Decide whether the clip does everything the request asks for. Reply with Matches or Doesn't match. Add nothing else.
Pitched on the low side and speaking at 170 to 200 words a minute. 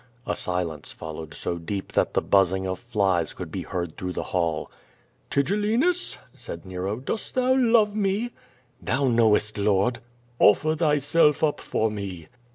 Doesn't match